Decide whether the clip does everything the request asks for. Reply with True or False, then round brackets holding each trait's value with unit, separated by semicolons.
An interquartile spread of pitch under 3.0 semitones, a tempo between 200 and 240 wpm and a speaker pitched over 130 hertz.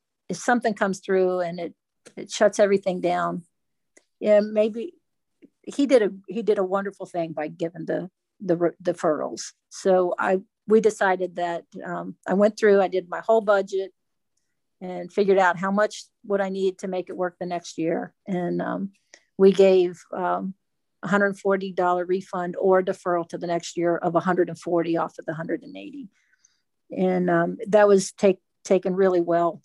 False (2.4 semitones; 170 wpm; 185 Hz)